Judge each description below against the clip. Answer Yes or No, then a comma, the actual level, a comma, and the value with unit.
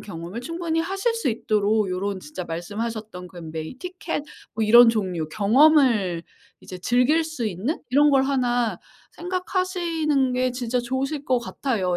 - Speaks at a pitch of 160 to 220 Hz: No, high, 245 Hz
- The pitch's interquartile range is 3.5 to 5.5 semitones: No, wide, 6.9 semitones